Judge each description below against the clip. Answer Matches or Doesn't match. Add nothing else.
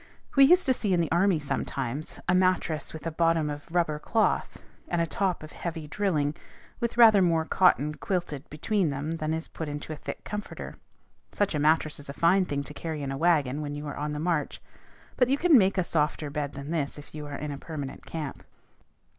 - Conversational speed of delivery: Doesn't match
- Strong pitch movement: Doesn't match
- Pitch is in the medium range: Matches